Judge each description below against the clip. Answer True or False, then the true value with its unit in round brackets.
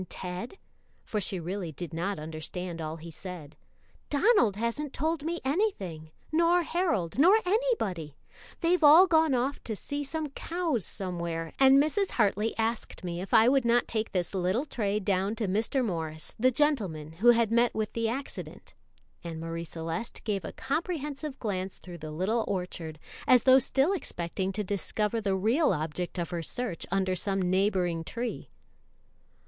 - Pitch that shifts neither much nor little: False (7.5 semitones)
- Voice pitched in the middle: False (210 Hz)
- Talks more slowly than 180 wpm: True (165 wpm)